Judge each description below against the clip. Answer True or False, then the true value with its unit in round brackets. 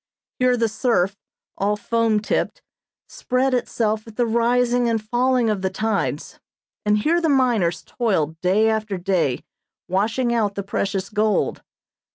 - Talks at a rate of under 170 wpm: True (145 wpm)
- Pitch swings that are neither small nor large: True (3.3 semitones)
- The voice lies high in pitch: True (220 Hz)